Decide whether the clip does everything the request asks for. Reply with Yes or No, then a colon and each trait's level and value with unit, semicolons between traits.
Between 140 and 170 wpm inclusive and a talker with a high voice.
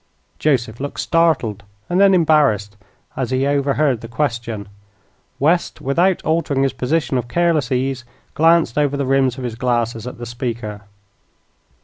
No: average, 145 wpm; low, 135 Hz